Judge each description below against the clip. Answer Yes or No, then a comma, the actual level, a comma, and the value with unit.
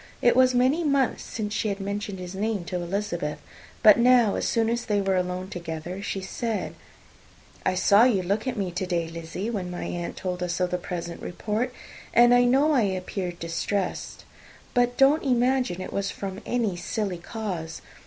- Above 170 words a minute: Yes, average, 185 wpm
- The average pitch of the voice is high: Yes, high, 200 Hz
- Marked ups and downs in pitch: No, average, 4.8 semitones